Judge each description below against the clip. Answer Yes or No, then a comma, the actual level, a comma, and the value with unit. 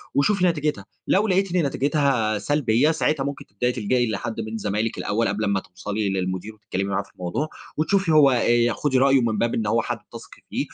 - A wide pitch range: Yes, wide, 5.8 semitones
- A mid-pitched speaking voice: No, low, 120 Hz